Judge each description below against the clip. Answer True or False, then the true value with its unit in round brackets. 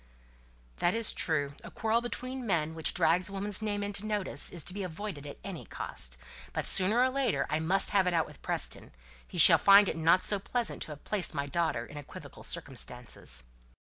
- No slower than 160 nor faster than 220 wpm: True (200 wpm)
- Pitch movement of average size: True (4.8 semitones)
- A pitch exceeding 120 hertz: True (190 Hz)